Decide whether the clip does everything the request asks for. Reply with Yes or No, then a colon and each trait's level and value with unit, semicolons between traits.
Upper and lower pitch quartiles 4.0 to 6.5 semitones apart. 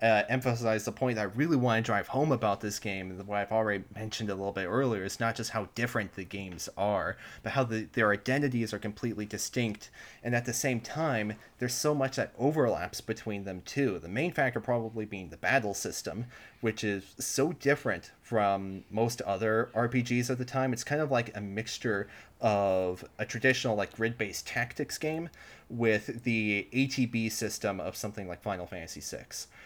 No: average, 3.4 semitones